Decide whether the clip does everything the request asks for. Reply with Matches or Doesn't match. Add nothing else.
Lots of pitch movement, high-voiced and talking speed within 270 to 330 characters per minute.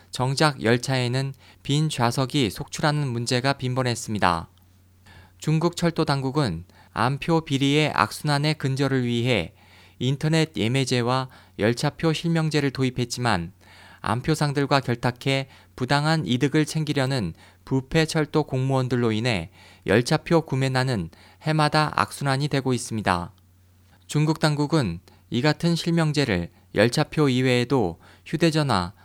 Doesn't match